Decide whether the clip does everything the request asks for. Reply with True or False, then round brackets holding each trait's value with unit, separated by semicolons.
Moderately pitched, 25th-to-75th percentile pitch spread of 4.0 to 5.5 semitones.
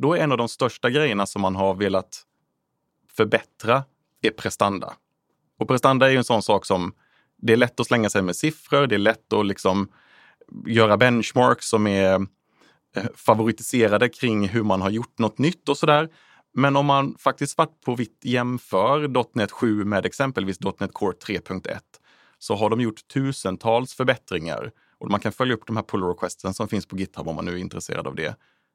False (115 Hz; 5.0 semitones)